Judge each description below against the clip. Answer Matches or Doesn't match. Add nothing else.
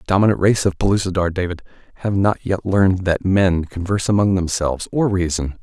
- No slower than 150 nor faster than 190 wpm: Matches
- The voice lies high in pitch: Doesn't match